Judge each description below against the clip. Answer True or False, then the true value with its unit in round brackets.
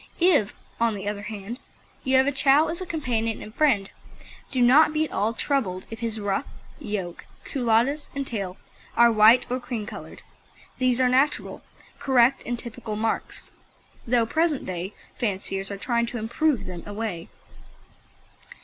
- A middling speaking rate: True (160 wpm)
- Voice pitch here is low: False (235 Hz)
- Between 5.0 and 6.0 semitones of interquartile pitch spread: False (4.1 semitones)